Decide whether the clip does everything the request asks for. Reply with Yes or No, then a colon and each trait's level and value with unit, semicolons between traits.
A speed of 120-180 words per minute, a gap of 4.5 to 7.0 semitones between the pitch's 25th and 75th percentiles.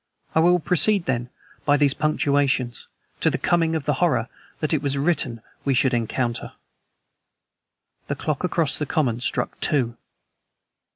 No: average, 150 wpm; average, 4.0 semitones